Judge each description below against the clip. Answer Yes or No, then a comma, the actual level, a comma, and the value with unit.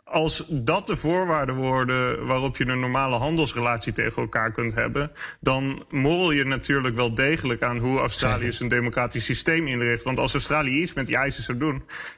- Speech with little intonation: No, average, 3.7 semitones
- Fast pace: No, average, 175 wpm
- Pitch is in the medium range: No, low, 130 Hz